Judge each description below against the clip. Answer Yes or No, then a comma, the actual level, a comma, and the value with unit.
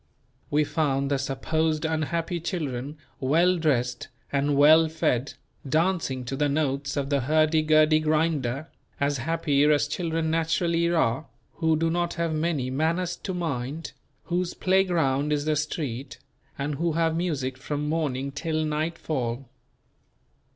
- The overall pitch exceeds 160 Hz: No, medium, 155 Hz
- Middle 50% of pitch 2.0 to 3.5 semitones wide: Yes, average, 2.9 semitones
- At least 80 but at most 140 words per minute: Yes, slow, 135 wpm